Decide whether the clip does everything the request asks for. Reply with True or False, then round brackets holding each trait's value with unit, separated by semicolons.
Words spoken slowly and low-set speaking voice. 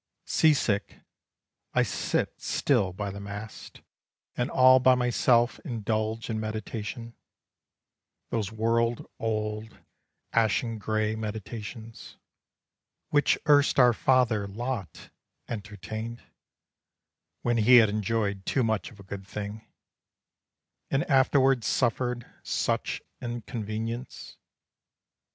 True (100 wpm; 115 Hz)